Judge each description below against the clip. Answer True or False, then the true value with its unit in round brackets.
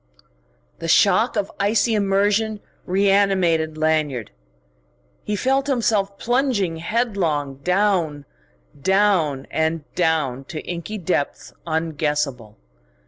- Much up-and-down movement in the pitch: False (4.7 semitones)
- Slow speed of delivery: True (90 wpm)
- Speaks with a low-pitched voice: False (180 Hz)